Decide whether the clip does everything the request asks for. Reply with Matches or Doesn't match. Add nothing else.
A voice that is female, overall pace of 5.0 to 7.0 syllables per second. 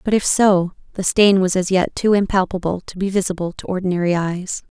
Matches